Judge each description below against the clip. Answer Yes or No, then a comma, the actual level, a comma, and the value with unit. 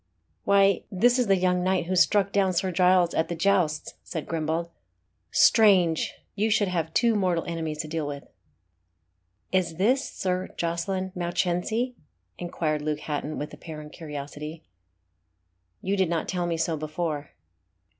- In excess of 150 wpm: No, average, 145 wpm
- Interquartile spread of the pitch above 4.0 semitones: No, average, 3.0 semitones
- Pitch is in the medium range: Yes, medium, 175 Hz